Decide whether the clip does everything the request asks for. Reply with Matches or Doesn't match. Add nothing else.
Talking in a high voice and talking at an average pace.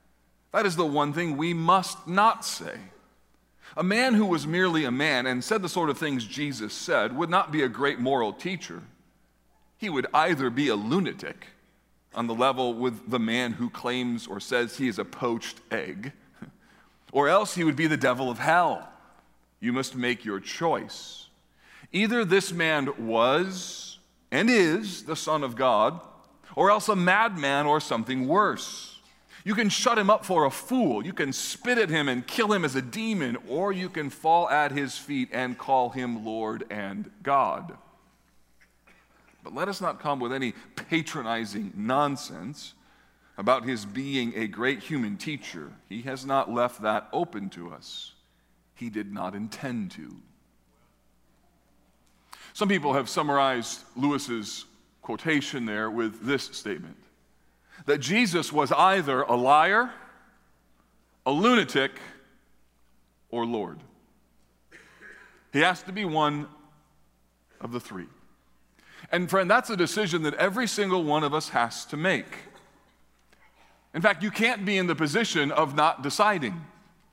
Doesn't match